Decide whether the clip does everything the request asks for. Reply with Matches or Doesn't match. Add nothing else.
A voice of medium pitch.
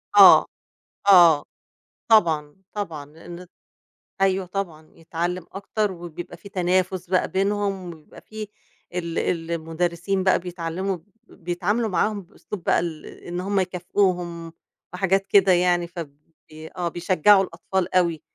Matches